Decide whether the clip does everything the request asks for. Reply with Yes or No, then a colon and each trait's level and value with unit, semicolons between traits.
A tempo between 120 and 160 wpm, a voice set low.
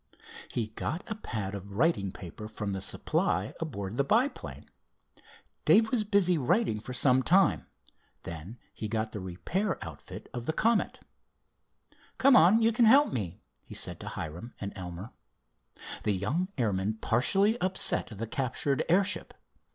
Yes: average, 150 wpm; low, 125 Hz